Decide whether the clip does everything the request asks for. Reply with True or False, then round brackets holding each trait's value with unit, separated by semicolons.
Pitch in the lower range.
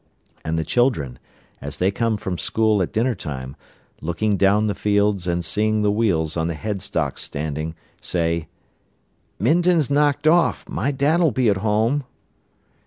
True (105 Hz)